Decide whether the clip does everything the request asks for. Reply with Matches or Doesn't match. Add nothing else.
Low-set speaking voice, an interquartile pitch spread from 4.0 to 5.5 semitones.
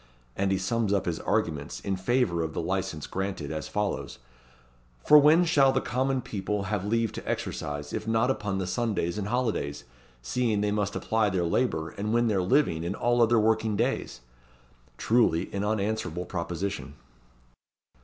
Matches